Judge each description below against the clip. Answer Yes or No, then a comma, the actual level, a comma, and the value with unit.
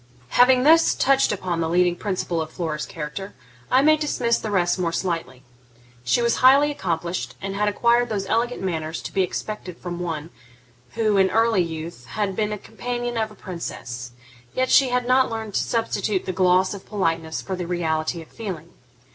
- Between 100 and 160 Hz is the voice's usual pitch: No, high, 190 Hz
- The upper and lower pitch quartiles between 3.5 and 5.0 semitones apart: No, wide, 5.4 semitones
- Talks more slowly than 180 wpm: No, average, 185 wpm